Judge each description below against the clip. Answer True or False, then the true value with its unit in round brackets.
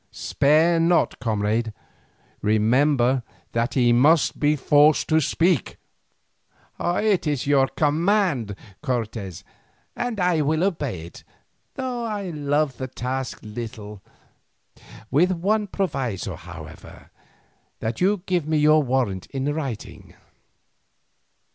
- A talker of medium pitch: True (145 Hz)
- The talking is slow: True (110 wpm)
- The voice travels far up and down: True (6.3 semitones)